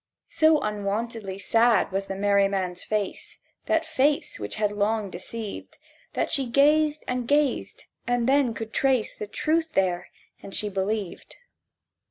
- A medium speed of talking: Yes, average, 145 wpm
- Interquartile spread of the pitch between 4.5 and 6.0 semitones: Yes, average, 5.0 semitones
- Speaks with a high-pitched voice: Yes, high, 220 Hz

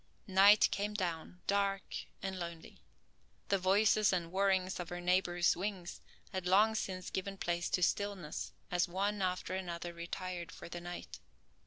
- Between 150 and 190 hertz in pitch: Yes, medium, 185 Hz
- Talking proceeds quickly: No, average, 150 wpm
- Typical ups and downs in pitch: No, narrow, 2.1 semitones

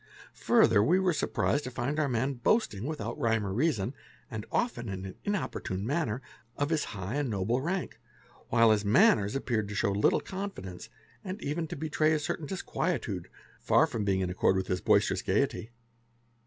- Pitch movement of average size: No, wide, 7.3 semitones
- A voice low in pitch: Yes, low, 120 Hz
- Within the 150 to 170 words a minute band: No, average, 180 wpm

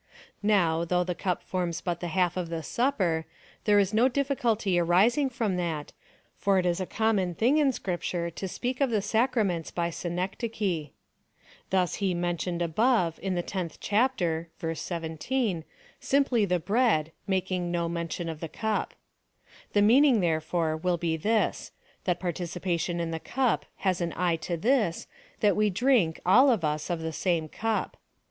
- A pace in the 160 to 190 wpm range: Yes, average, 175 wpm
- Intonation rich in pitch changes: No, average, 4.4 semitones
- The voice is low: No, medium, 180 Hz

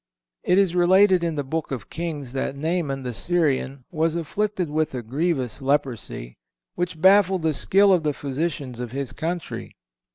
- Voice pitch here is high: No, medium, 155 Hz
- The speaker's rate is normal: Yes, average, 170 wpm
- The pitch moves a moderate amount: Yes, average, 4.6 semitones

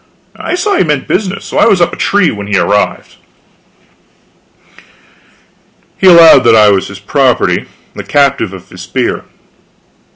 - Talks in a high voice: No, low, 135 Hz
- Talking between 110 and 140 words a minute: No, average, 155 wpm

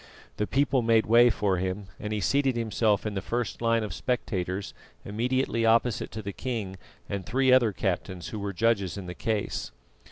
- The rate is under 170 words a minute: No, average, 185 wpm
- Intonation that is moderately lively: Yes, average, 3.1 semitones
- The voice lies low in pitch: Yes, low, 110 Hz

